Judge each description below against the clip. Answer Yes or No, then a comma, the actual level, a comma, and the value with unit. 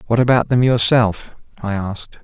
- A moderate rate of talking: Yes, average, 160 wpm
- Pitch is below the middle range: Yes, low, 115 Hz